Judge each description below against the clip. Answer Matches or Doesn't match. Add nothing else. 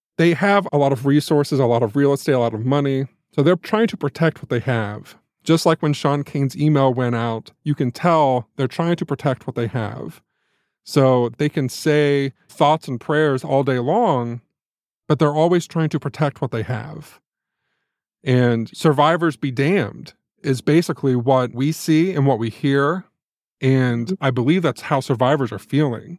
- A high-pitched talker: Doesn't match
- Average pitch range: Matches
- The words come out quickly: Doesn't match